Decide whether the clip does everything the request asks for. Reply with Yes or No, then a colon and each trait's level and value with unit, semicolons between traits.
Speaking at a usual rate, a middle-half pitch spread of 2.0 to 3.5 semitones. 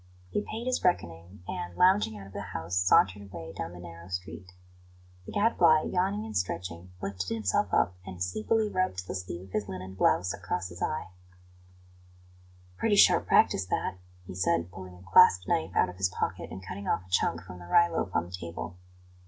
Yes: average, 195 wpm; average, 2.8 semitones